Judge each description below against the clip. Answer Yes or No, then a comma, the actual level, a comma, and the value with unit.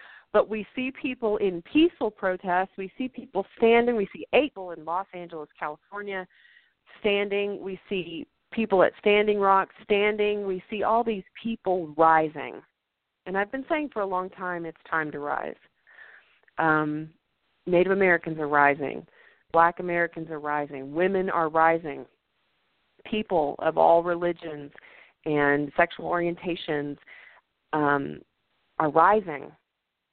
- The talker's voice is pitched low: No, medium, 180 Hz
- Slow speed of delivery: Yes, slow, 130 wpm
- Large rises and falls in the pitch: No, average, 4.4 semitones